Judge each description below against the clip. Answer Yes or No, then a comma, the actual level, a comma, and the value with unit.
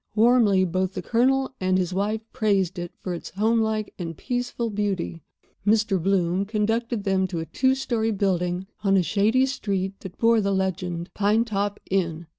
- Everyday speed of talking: Yes, average, 170 wpm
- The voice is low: No, high, 200 Hz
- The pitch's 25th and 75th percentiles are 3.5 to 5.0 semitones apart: No, average, 3.1 semitones